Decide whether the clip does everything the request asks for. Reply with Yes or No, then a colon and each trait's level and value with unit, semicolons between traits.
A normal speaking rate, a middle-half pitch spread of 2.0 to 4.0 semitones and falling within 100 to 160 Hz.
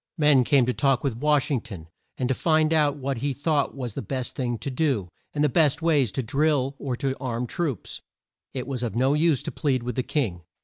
No: fast, 230 wpm; average, 3.2 semitones; low, 135 Hz